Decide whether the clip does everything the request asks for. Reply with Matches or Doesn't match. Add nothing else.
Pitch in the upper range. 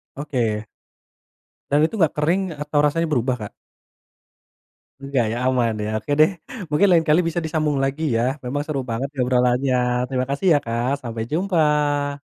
Doesn't match